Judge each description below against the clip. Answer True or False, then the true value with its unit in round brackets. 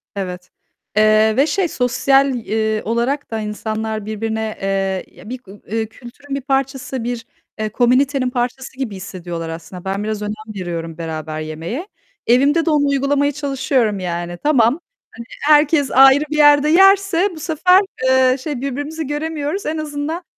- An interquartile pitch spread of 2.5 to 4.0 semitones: False (5.4 semitones)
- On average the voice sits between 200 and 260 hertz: True (250 Hz)